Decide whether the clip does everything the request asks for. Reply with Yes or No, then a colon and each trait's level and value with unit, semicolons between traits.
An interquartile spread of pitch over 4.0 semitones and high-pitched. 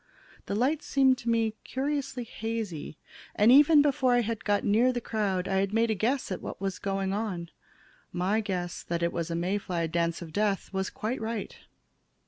Yes: average, 4.5 semitones; high, 210 Hz